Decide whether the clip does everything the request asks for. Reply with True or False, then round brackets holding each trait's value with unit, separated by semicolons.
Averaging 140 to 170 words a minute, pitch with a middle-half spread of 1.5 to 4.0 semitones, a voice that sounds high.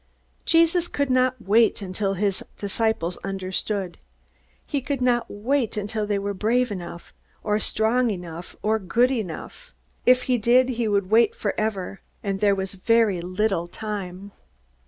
True (145 wpm; 3.7 semitones; 210 Hz)